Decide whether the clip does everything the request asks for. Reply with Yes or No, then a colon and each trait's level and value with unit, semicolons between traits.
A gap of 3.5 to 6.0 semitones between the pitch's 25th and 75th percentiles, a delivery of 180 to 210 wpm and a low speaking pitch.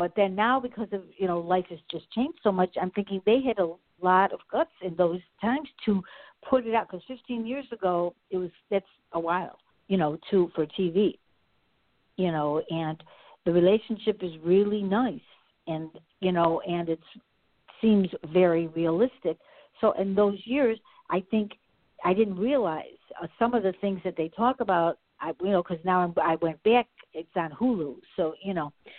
No: average, 4.7 semitones; average, 190 wpm; high, 190 Hz